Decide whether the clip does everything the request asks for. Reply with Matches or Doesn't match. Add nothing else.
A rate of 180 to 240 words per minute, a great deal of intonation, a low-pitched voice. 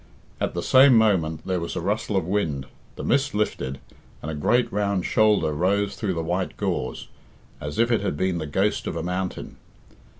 Doesn't match